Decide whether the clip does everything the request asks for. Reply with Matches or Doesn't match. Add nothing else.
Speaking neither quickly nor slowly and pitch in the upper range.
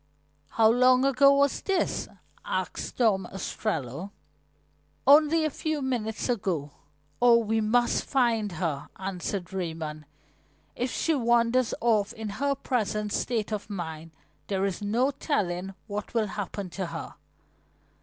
Doesn't match